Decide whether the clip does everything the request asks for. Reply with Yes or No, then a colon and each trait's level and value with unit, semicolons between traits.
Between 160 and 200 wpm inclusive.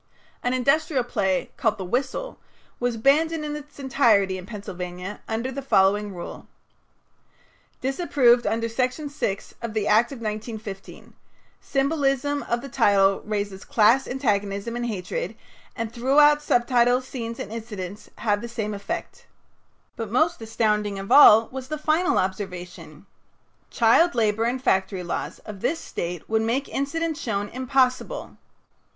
No: average, 140 wpm